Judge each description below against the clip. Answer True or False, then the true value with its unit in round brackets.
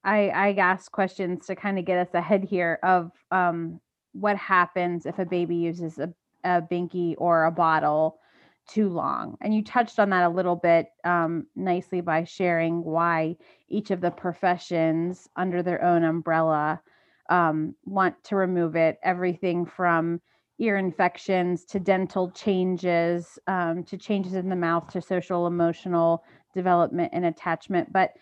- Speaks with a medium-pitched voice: True (175 Hz)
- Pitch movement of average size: False (1.9 semitones)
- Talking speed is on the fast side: False (155 wpm)